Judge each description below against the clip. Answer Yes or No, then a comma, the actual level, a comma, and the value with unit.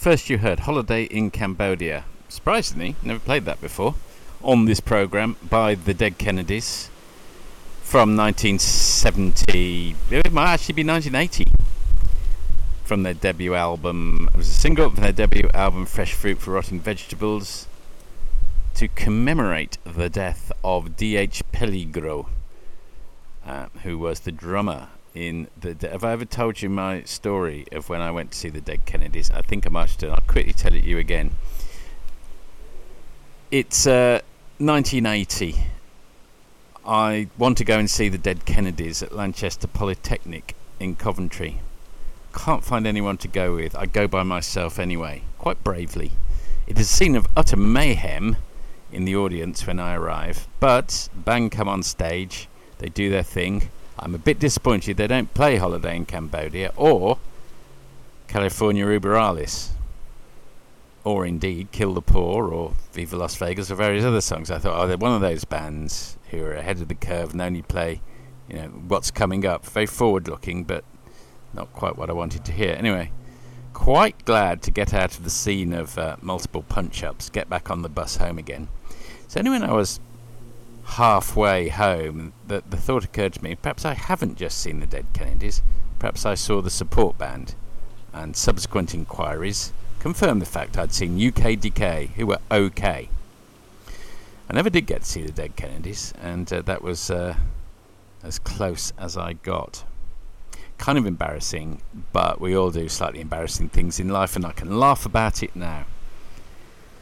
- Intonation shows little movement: No, average, 4.1 semitones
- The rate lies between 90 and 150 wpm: No, average, 165 wpm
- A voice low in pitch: Yes, very low, 95 Hz